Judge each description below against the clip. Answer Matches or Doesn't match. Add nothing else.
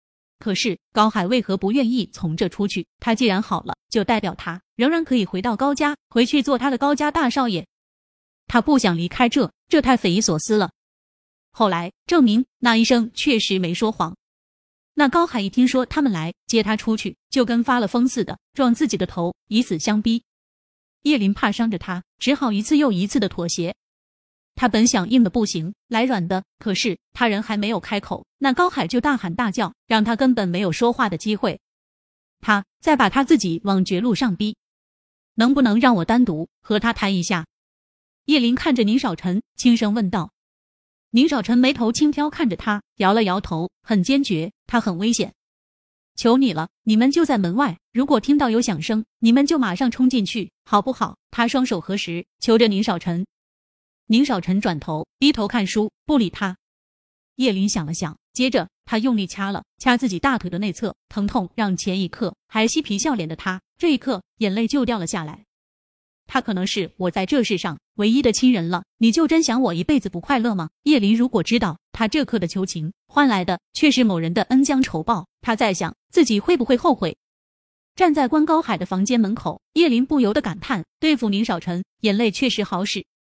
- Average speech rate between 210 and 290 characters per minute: Matches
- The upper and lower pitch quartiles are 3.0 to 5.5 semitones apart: Matches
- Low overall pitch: Doesn't match